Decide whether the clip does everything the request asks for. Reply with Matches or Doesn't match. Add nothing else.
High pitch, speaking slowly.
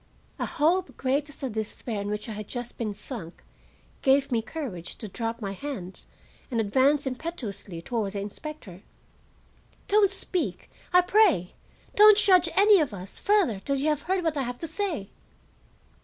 Doesn't match